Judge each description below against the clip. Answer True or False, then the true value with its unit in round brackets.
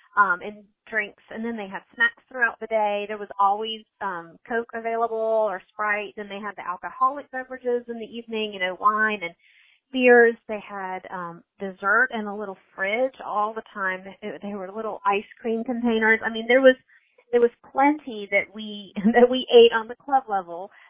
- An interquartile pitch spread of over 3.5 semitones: False (2.8 semitones)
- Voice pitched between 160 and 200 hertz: False (215 Hz)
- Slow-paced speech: False (190 wpm)